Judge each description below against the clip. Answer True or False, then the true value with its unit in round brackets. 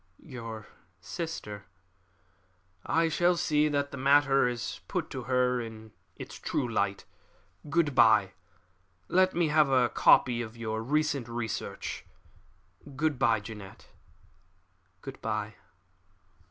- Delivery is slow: True (120 wpm)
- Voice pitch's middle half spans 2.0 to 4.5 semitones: False (5.0 semitones)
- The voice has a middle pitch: False (125 Hz)